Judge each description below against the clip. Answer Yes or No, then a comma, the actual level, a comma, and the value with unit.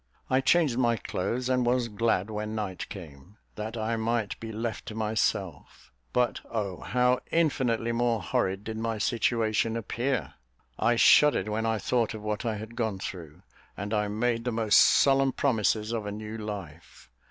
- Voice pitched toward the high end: No, low, 110 Hz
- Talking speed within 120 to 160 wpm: No, average, 170 wpm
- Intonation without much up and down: Yes, narrow, 2.2 semitones